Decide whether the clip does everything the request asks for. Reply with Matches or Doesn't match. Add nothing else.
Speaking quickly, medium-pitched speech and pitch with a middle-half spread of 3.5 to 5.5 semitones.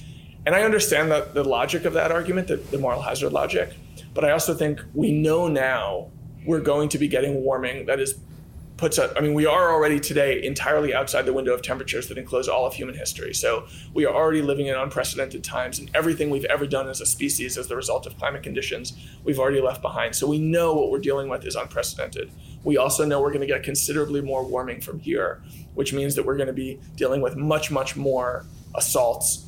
Doesn't match